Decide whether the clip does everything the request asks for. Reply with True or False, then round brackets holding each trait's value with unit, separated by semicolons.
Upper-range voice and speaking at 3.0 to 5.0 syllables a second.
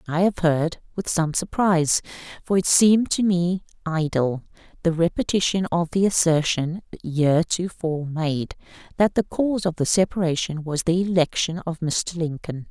False (170 Hz; 4.8 syllables/s)